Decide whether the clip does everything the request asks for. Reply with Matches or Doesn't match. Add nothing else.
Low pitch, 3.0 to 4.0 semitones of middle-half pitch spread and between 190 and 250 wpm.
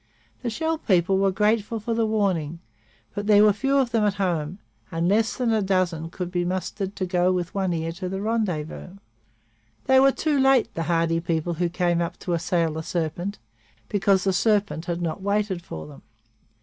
Doesn't match